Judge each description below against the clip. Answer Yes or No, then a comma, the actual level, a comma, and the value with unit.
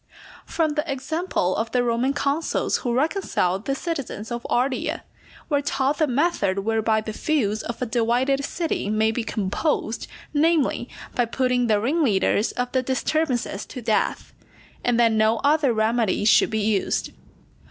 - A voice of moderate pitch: No, high, 245 Hz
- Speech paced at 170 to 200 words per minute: No, average, 160 wpm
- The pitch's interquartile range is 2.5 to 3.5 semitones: No, average, 4.4 semitones